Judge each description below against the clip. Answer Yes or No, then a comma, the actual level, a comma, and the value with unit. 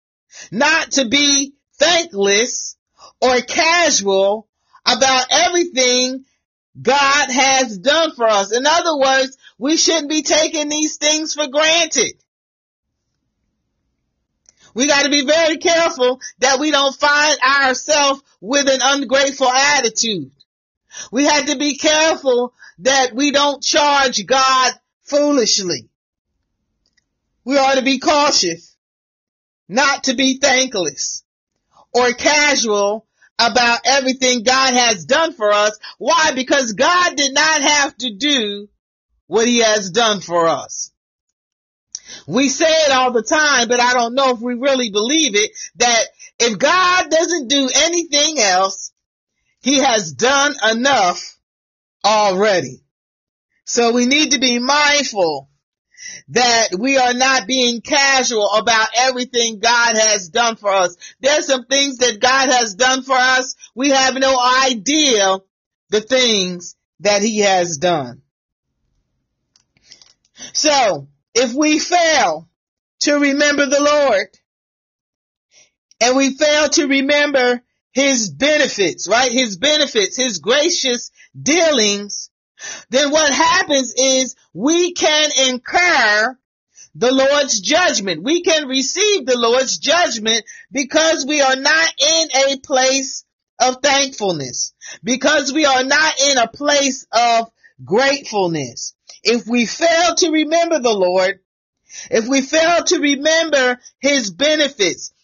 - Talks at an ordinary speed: No, slow, 125 wpm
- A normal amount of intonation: Yes, average, 3.9 semitones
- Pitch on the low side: No, very high, 270 Hz